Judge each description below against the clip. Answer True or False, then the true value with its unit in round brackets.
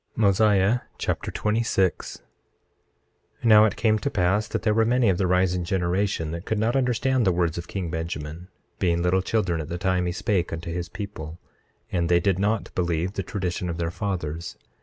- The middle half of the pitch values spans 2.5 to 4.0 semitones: True (3.6 semitones)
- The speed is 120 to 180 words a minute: False (190 wpm)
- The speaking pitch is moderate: False (95 Hz)